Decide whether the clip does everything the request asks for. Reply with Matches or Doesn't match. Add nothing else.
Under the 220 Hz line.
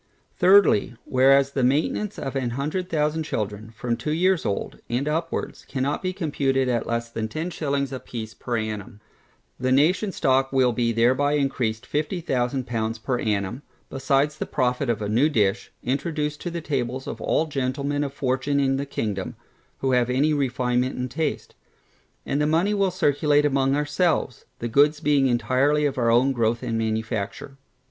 Matches